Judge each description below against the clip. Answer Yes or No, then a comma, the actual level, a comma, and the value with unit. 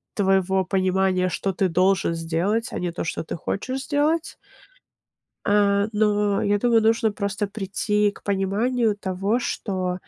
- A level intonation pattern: Yes, narrow, 2.3 semitones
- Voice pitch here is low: No, high, 200 Hz